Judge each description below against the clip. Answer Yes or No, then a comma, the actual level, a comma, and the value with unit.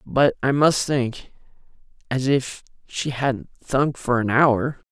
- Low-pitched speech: Yes, low, 130 Hz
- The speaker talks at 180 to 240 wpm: No, average, 145 wpm